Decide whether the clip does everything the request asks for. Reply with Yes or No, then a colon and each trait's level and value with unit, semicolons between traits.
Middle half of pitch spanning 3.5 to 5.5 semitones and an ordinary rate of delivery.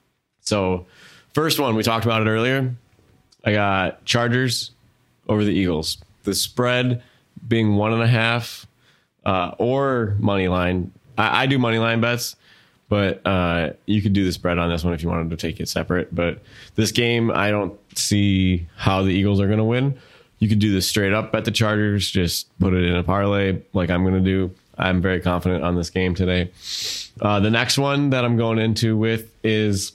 Yes: average, 3.8 semitones; average, 195 wpm